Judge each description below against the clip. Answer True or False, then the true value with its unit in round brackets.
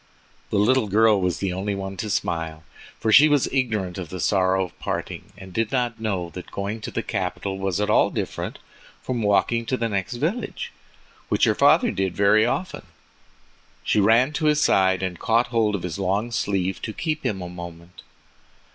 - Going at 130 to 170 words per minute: False (190 wpm)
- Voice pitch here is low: True (100 Hz)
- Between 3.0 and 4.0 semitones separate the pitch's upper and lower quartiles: True (3.7 semitones)